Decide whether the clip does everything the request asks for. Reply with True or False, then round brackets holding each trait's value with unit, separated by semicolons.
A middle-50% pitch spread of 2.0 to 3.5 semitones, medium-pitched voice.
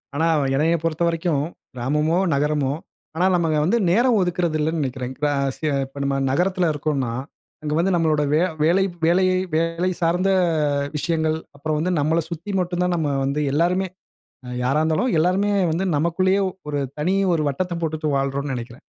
True (3.2 semitones; 160 Hz)